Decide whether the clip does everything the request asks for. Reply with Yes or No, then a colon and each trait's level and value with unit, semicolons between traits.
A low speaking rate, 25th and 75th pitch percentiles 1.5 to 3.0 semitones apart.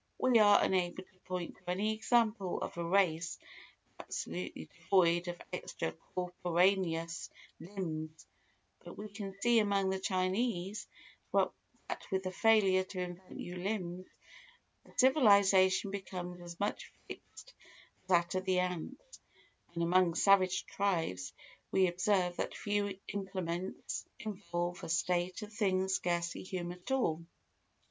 Yes: slow, 130 wpm; narrow, 2.4 semitones